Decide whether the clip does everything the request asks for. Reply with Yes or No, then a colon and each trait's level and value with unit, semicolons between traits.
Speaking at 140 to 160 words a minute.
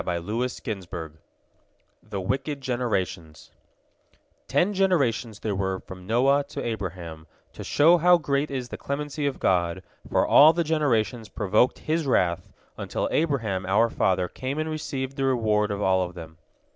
Yes: average, 150 wpm